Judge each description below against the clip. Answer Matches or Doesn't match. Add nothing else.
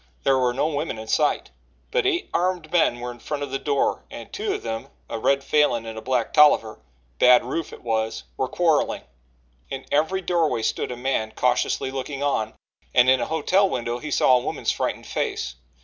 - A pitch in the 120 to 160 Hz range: Matches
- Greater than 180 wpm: Matches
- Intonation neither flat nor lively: Matches